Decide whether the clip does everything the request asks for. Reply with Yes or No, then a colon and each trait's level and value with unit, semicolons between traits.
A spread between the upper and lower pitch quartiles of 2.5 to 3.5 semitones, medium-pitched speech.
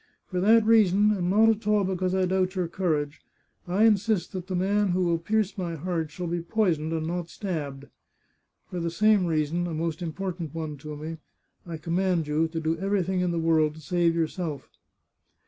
Yes: average, 2.8 semitones; medium, 175 Hz